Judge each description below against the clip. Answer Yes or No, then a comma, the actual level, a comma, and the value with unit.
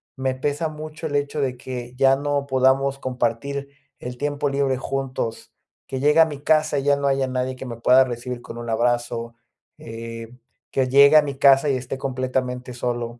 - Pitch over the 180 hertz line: No, low, 130 Hz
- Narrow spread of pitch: Yes, narrow, 2.2 semitones